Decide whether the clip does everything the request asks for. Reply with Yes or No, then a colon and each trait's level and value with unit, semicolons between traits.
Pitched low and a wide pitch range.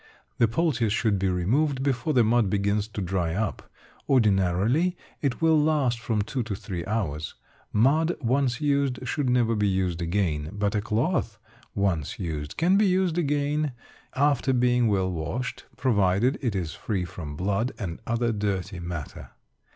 Yes: low, 110 Hz; wide, 6.0 semitones